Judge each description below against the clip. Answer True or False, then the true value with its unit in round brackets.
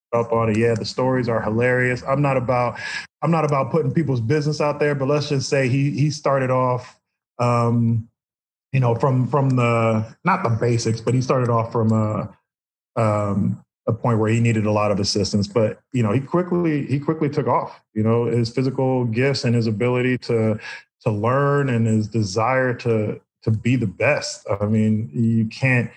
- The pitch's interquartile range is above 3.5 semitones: False (3.1 semitones)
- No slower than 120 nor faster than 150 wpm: False (195 wpm)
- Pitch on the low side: True (120 Hz)